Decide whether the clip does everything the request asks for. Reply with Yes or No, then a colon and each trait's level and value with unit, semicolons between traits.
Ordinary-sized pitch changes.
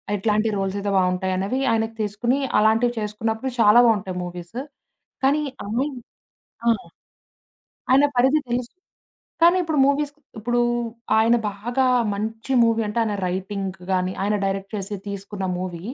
Yes: average, 3.7 semitones